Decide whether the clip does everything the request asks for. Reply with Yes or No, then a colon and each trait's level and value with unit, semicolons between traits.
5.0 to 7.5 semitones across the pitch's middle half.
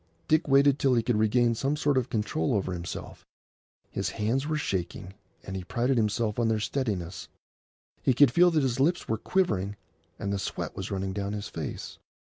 Yes: wide, 5.4 semitones